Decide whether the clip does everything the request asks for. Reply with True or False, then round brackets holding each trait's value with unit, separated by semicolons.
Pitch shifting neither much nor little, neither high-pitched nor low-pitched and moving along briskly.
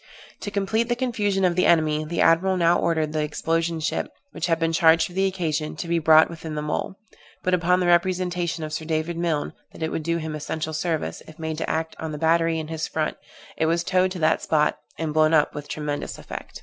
False (2.0 semitones; 165 Hz; 230 wpm)